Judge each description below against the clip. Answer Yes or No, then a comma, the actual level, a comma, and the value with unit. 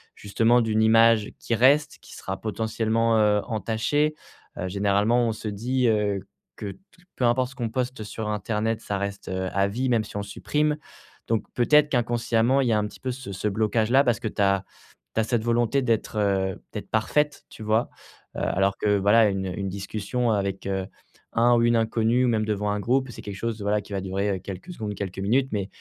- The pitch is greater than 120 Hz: No, low, 110 Hz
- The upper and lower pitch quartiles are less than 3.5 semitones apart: Yes, average, 2.8 semitones